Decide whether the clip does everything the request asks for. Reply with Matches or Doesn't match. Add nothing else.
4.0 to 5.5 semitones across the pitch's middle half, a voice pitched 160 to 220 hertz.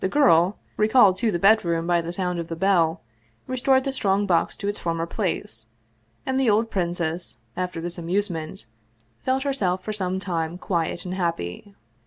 Doesn't match